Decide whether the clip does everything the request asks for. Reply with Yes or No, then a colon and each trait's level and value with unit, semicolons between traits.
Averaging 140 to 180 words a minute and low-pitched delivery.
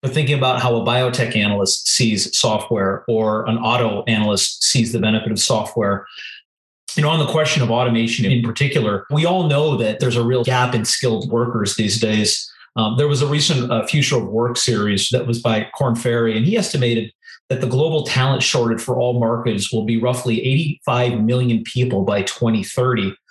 No: average, 190 wpm; low, 120 Hz